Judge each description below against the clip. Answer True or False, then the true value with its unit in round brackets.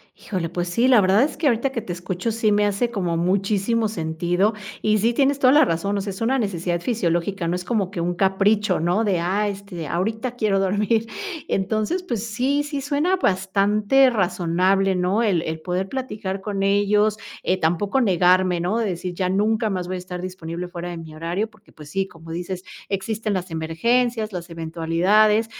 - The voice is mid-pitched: False (195 Hz)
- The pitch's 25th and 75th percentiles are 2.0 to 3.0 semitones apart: False (3.7 semitones)